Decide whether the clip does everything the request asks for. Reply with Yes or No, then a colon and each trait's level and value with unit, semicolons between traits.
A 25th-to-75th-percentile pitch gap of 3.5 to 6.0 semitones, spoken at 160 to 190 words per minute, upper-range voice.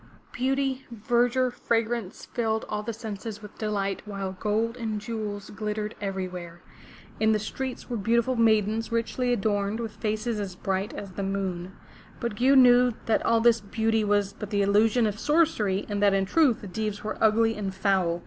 No: narrow, 2.5 semitones; average, 175 wpm; high, 215 Hz